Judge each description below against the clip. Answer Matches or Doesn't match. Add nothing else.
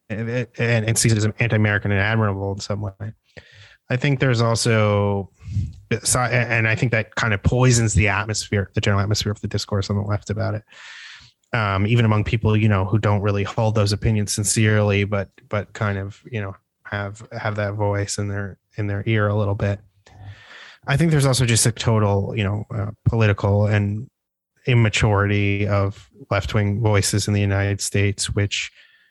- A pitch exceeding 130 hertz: Doesn't match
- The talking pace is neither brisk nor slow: Matches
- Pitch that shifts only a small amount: Matches